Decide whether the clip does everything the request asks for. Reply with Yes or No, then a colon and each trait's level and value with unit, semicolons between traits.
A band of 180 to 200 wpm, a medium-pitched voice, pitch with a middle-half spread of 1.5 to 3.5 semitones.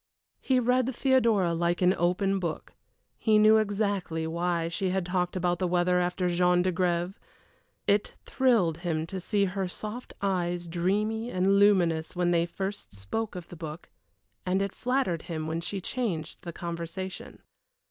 No: average, 155 wpm; medium, 180 Hz; average, 2.9 semitones